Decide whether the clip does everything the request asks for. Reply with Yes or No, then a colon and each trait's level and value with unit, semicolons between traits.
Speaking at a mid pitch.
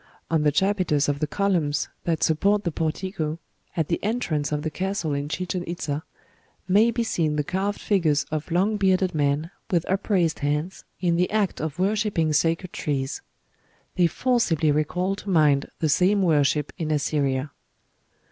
Yes: medium, 165 Hz